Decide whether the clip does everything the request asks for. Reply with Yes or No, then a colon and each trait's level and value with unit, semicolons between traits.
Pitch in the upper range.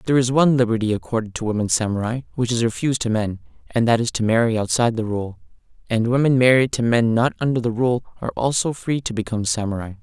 No: low, 115 Hz